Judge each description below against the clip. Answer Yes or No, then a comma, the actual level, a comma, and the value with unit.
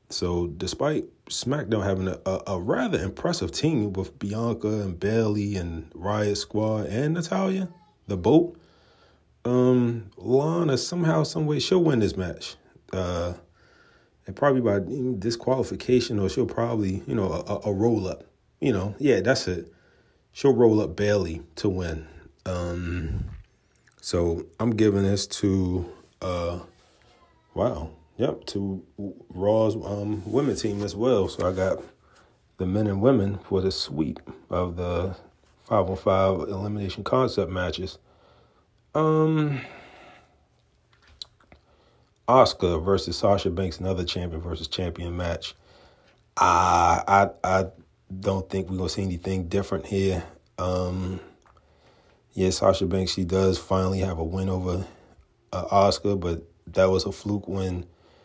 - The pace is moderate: No, slow, 130 wpm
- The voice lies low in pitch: Yes, very low, 95 Hz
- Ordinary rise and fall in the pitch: Yes, average, 3.4 semitones